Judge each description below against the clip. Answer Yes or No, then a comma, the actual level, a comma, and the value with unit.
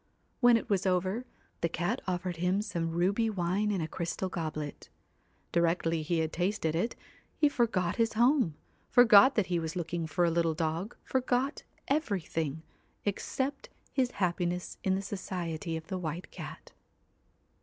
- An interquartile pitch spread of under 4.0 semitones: No, average, 4.4 semitones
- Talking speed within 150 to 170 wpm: Yes, average, 155 wpm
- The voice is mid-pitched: Yes, medium, 180 Hz